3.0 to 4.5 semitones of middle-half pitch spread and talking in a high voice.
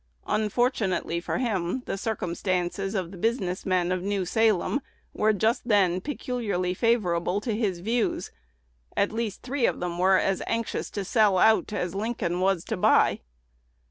Yes: average, 3.8 semitones; high, 200 Hz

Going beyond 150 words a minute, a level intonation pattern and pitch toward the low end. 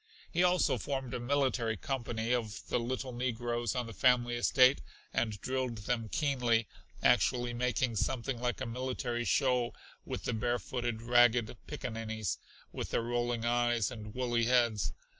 No: average, 145 wpm; narrow, 1.5 semitones; low, 120 Hz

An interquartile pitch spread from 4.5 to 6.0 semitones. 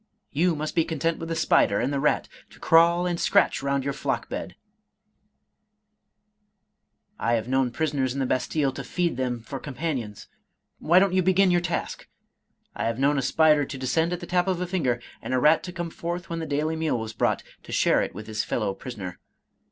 Yes: average, 4.8 semitones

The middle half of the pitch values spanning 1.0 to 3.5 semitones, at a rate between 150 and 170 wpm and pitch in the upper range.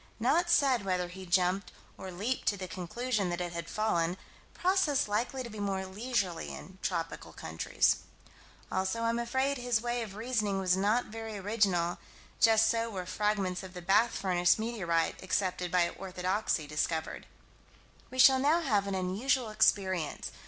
No: average, 4.2 semitones; average, 160 wpm; high, 200 Hz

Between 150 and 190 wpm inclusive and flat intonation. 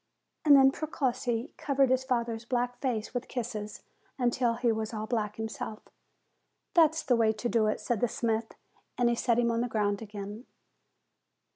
Yes: average, 170 wpm; narrow, 2.3 semitones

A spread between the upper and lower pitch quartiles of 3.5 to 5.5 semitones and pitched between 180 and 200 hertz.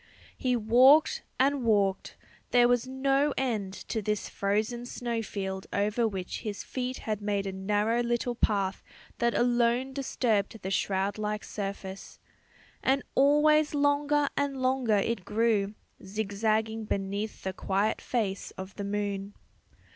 No: average, 3.9 semitones; high, 220 Hz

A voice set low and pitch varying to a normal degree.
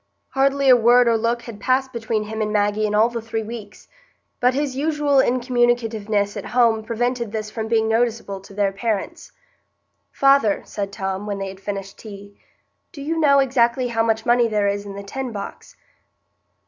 No: high, 225 Hz; average, 3.1 semitones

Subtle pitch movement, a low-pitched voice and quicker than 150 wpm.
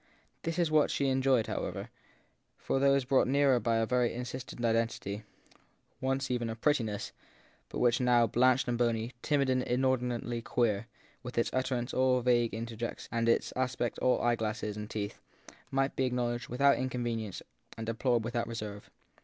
Yes: narrow, 2.1 semitones; low, 120 Hz; average, 165 wpm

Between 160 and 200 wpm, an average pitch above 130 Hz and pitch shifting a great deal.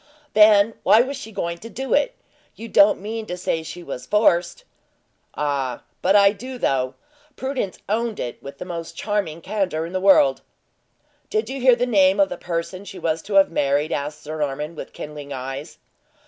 Yes: average, 190 wpm; medium, 185 Hz; wide, 6.1 semitones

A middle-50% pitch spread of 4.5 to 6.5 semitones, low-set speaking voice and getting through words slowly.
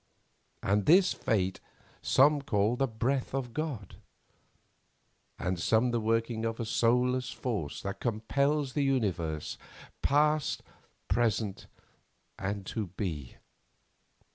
Yes: average, 5.0 semitones; low, 115 Hz; slow, 110 wpm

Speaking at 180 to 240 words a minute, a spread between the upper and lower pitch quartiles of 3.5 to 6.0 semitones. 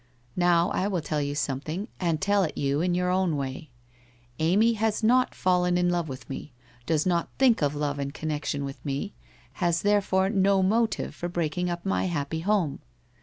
Yes: average, 190 wpm; average, 4.4 semitones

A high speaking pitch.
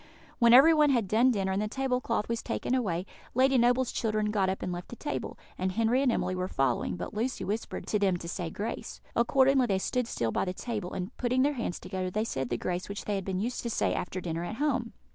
Yes: high, 215 Hz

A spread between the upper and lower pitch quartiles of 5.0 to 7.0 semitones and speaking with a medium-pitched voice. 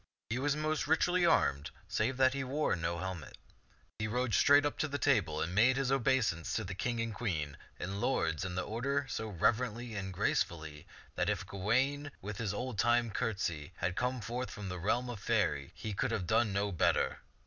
No: wide, 5.6 semitones; low, 110 Hz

